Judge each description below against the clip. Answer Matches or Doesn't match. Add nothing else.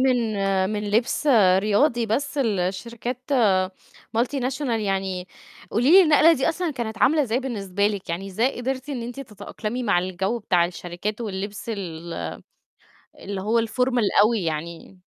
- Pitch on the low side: Doesn't match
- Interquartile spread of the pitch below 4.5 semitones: Doesn't match